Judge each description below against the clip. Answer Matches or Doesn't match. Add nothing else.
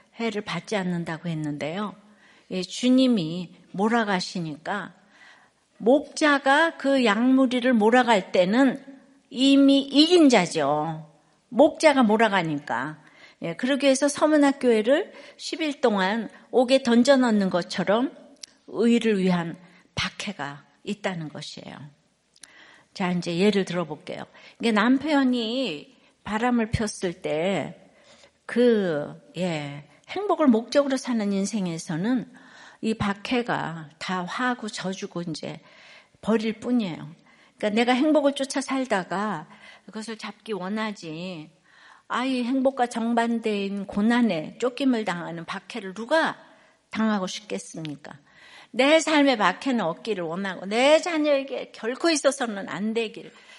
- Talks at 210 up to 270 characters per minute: Matches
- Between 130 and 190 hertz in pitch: Doesn't match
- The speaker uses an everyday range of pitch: Doesn't match